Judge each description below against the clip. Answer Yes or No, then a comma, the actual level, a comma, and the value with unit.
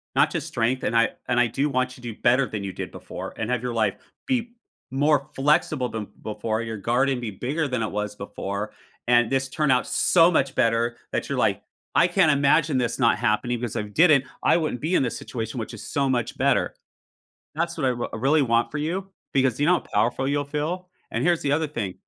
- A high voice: No, low, 130 Hz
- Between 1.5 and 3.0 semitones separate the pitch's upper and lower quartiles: No, average, 4.3 semitones